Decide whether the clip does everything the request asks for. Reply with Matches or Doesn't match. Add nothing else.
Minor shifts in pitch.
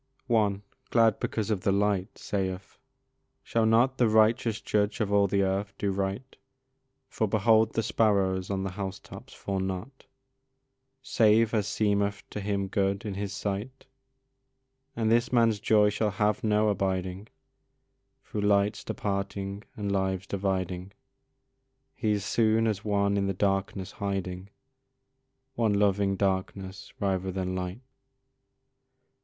Matches